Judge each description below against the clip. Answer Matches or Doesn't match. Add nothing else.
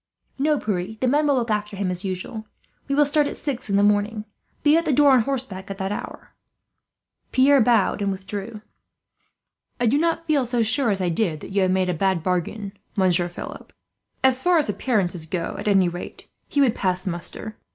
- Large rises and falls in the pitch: Matches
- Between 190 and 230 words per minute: Matches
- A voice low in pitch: Doesn't match